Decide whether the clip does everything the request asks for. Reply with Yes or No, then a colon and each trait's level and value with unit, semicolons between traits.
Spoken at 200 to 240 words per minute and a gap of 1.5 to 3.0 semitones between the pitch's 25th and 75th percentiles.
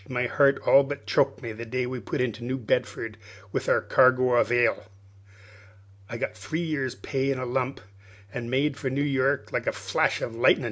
Yes: fast, 205 wpm; narrow, 2.4 semitones